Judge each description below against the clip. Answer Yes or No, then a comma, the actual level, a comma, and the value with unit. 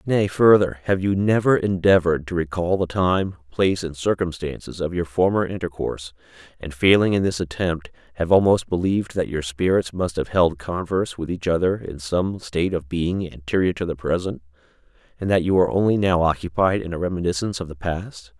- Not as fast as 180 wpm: No, average, 185 wpm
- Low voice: Yes, very low, 90 Hz